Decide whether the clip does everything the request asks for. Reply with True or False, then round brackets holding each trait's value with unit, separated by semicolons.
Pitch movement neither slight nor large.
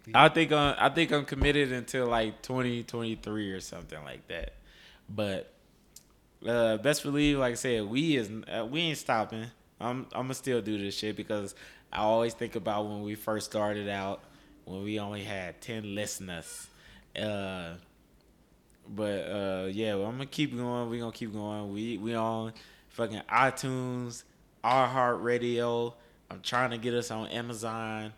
True (3.0 semitones)